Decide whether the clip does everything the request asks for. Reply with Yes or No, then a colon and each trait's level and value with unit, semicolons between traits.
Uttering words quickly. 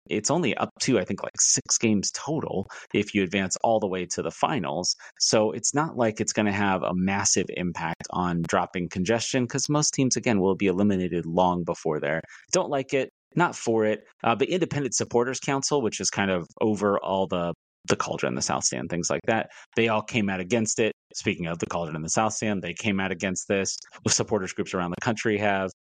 Yes: fast, 220 wpm